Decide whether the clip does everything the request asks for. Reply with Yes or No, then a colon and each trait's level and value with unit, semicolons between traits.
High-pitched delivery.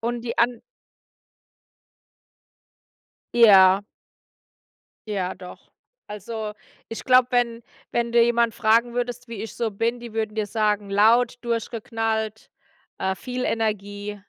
Yes: high, 225 Hz